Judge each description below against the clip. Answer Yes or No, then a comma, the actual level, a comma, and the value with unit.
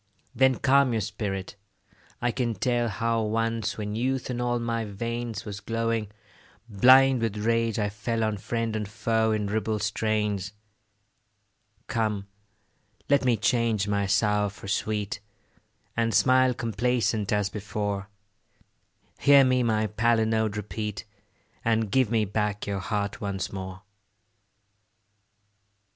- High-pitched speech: No, low, 110 Hz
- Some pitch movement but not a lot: No, narrow, 2.2 semitones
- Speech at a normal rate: No, slow, 125 wpm